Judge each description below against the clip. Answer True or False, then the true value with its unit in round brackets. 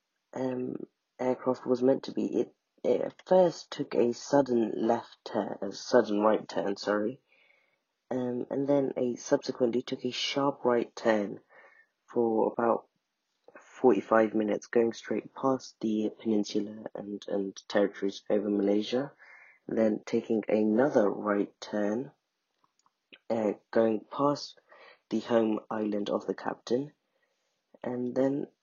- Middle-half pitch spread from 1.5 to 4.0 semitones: True (3.4 semitones)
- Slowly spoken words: True (125 wpm)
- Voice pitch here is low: True (115 Hz)